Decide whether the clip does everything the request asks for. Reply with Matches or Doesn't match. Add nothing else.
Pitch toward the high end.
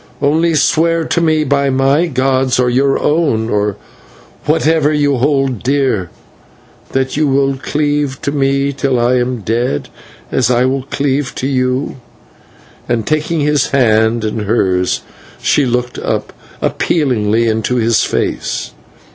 Doesn't match